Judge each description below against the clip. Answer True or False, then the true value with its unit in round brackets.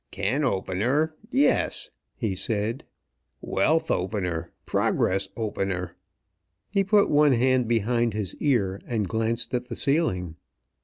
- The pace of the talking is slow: True (115 wpm)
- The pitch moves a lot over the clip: True (5.9 semitones)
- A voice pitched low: True (115 Hz)